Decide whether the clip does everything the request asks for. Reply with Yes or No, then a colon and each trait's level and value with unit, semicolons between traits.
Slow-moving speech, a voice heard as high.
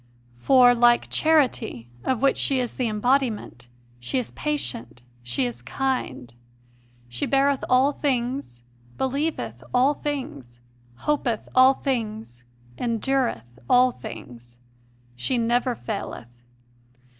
Yes: slow, 115 wpm; high, 245 Hz